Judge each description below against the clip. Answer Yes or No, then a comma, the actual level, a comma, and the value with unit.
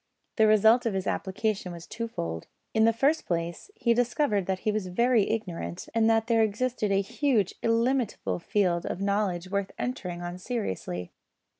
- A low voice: No, high, 210 Hz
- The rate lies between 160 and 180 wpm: Yes, average, 165 wpm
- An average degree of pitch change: Yes, average, 4.0 semitones